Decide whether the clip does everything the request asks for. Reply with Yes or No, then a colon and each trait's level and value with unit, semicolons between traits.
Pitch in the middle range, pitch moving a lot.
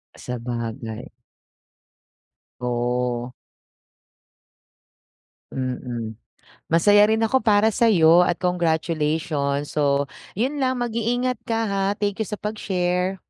Yes: medium, 175 Hz; wide, 8.7 semitones